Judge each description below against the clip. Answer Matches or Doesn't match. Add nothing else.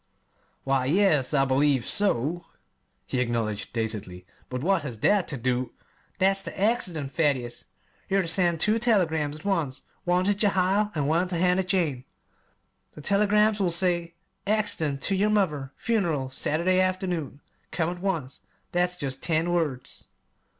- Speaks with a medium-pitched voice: Matches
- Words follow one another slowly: Doesn't match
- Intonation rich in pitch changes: Matches